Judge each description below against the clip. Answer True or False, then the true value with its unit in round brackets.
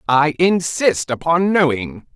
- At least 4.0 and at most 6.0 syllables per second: False (3.7 syllables/s)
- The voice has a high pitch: False (155 Hz)